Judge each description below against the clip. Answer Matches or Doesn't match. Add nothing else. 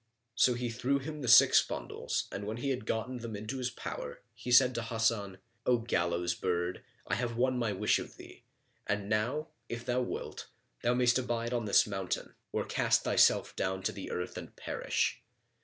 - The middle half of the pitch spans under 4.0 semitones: Matches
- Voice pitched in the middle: Doesn't match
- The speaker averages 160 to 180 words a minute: Doesn't match